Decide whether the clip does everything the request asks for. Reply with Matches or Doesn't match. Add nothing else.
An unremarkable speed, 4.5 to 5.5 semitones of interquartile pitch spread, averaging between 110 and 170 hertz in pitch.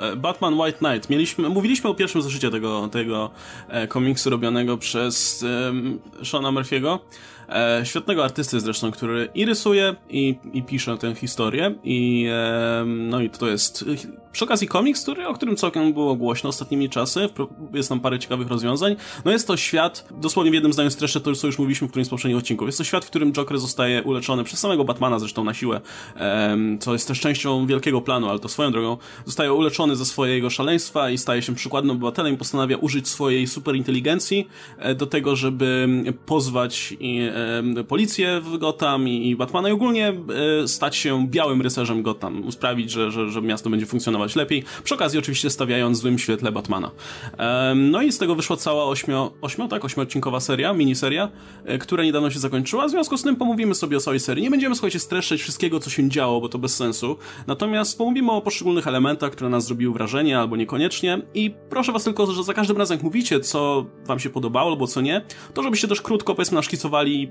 Doesn't match